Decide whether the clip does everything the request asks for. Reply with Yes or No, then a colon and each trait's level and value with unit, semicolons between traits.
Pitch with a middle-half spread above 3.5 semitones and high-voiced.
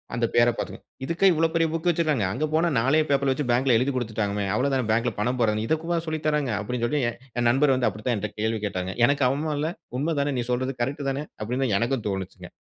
No: average, 4.7 semitones; low, 130 Hz